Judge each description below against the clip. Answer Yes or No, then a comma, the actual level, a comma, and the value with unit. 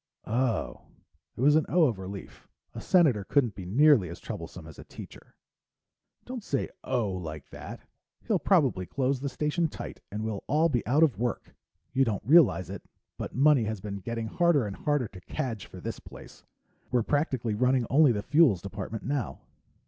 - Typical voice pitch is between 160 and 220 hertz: No, low, 120 Hz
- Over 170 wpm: Yes, average, 180 wpm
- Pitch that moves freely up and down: Yes, wide, 6.2 semitones